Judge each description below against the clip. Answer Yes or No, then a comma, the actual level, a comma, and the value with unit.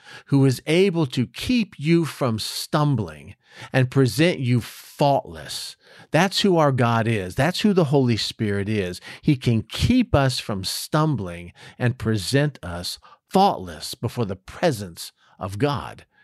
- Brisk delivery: No, average, 140 wpm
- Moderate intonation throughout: No, wide, 5.9 semitones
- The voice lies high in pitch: No, low, 130 Hz